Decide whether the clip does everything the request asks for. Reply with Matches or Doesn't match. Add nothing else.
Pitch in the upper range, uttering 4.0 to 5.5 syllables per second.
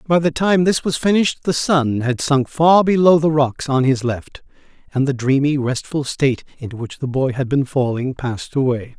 Doesn't match